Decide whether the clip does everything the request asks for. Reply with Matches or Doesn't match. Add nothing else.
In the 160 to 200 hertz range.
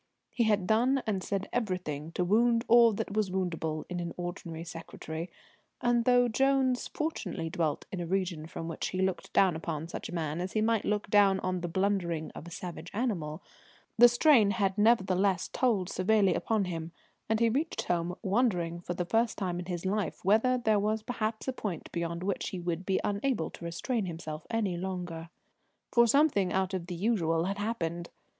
Matches